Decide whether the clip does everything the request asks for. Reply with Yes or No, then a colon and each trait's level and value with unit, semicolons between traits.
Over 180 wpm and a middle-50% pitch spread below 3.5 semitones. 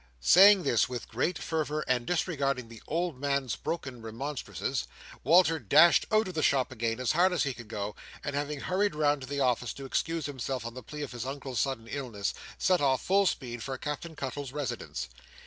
No: average, 200 wpm; average, 4.2 semitones